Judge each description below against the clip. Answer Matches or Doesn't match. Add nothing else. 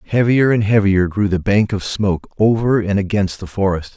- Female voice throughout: Doesn't match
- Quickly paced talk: Doesn't match